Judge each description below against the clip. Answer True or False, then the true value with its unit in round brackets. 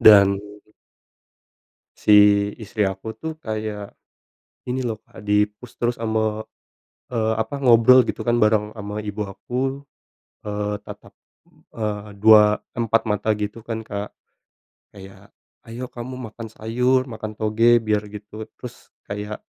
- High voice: False (110 Hz)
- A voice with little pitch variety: True (1.9 semitones)